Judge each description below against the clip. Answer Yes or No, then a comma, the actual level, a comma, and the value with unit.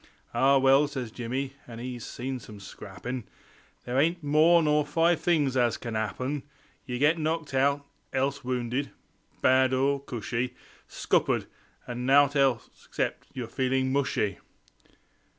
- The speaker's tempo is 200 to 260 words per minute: No, slow, 135 wpm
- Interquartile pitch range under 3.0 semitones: Yes, narrow, 2.5 semitones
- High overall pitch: No, low, 130 Hz